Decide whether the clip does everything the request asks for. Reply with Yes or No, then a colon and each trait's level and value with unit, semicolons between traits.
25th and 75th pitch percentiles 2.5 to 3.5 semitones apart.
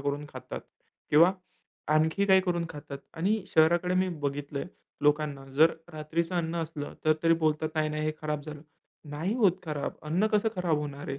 Yes: average, 2.8 semitones